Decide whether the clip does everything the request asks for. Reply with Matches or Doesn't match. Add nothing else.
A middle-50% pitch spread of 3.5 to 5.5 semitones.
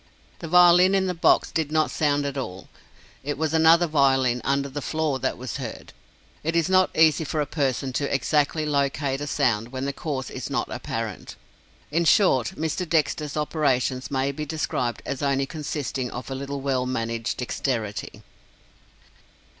Doesn't match